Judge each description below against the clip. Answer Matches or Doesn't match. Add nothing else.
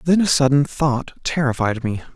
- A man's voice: Matches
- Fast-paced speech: Doesn't match